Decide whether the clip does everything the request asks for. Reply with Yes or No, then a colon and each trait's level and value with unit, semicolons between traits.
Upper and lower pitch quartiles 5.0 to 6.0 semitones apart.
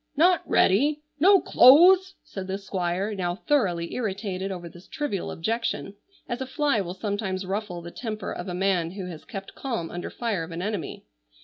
Yes: wide, 5.4 semitones